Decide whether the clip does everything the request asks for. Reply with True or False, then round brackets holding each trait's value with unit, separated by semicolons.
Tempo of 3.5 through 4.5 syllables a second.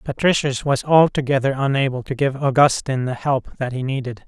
False (5.6 syllables/s)